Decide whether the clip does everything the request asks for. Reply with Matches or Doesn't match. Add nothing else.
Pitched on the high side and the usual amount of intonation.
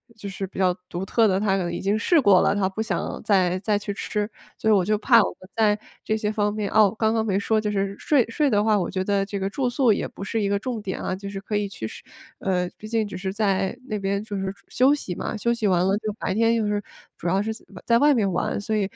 Doesn't match